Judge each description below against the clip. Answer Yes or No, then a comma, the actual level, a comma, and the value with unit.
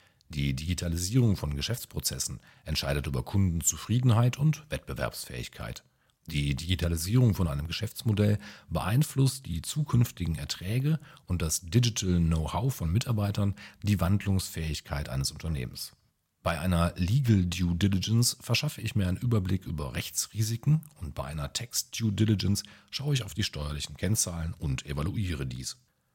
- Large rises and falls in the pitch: Yes, wide, 6.2 semitones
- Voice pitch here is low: Yes, very low, 95 Hz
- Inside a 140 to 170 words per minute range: No, slow, 125 wpm